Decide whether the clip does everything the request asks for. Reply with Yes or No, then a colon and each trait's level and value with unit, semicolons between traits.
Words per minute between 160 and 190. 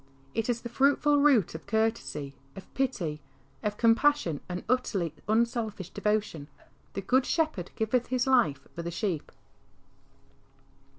No: slow, 135 wpm